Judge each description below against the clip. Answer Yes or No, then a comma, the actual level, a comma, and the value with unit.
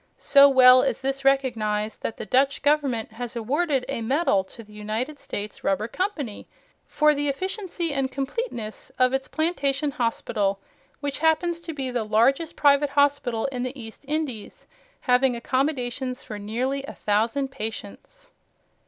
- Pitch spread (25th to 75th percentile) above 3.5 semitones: Yes, average, 4.1 semitones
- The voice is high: Yes, very high, 265 Hz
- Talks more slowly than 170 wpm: Yes, average, 150 wpm